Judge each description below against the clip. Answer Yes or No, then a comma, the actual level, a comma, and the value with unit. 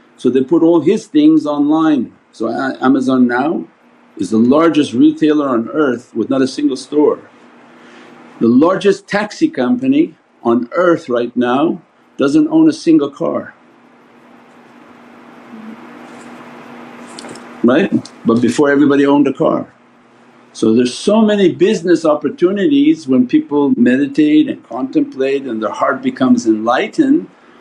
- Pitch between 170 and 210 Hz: Yes, medium, 185 Hz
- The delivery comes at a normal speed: No, slow, 125 wpm